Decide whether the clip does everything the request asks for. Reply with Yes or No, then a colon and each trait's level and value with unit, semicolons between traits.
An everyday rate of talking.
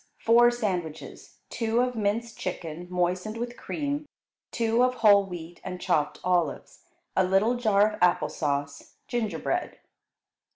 No: slow, 130 wpm